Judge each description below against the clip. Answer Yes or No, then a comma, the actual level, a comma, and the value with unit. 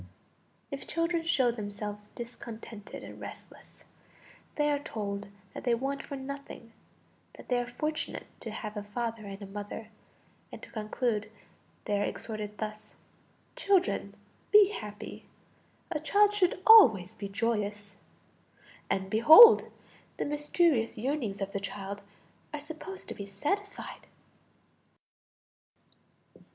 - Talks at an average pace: No, slow, 125 wpm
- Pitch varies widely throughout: Yes, wide, 6.3 semitones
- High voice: Yes, high, 230 Hz